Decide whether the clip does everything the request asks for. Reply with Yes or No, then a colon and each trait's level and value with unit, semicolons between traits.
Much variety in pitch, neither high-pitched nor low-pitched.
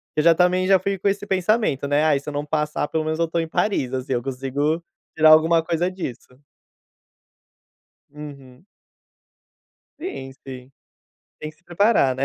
No: average, 4.5 semitones; medium, 155 Hz